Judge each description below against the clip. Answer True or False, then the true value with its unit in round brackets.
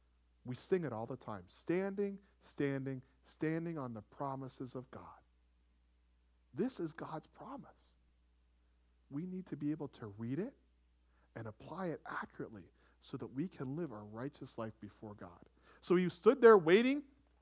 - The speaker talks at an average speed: True (155 wpm)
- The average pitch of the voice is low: True (125 Hz)